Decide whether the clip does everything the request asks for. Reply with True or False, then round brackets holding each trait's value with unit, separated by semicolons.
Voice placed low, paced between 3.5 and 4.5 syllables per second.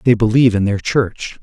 False (110 Hz; 5.4 syllables/s)